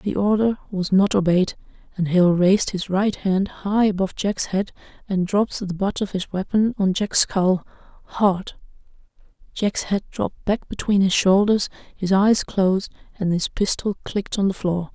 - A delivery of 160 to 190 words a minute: Yes, average, 170 wpm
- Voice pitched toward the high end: Yes, high, 195 Hz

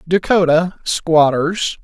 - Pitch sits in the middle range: Yes, medium, 170 Hz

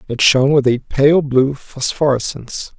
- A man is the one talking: Yes, male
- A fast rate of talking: No, average, 150 wpm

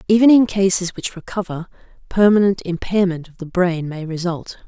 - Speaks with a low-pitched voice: No, medium, 185 Hz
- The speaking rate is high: No, average, 155 wpm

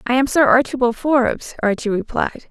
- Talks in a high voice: Yes, very high, 250 Hz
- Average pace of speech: Yes, average, 170 wpm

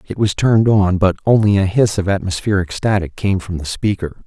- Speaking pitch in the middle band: No, very low, 95 Hz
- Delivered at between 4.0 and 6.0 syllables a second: Yes, 5.5 syllables/s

